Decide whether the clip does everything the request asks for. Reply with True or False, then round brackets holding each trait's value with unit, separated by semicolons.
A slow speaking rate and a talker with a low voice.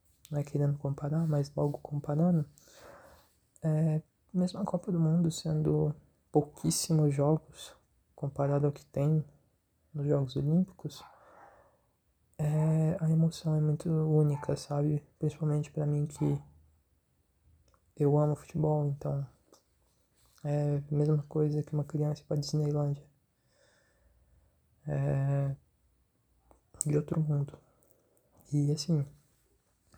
False (105 wpm; 145 Hz)